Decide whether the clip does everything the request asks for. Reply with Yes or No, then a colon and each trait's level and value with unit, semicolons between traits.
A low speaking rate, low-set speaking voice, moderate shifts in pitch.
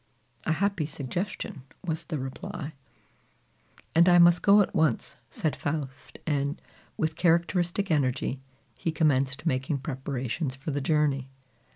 No: slow, 130 wpm; medium, 155 Hz; average, 4.1 semitones